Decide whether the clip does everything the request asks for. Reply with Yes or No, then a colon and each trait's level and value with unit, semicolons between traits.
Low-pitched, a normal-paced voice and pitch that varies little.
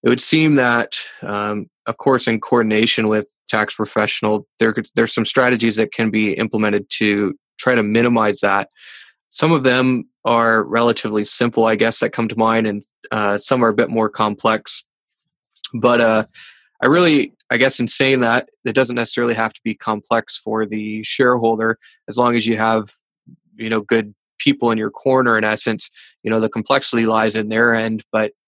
Yes: low, 115 Hz; average, 185 wpm; narrow, 1.7 semitones